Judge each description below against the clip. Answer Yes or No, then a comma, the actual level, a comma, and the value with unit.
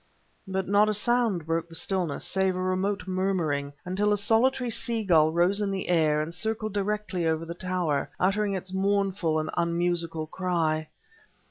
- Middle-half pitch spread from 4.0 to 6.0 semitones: No, average, 3.4 semitones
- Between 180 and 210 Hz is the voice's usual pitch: Yes, medium, 185 Hz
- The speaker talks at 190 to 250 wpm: No, average, 165 wpm